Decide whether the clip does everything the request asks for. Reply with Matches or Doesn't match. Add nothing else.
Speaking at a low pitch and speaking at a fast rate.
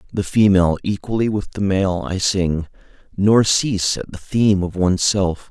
Doesn't match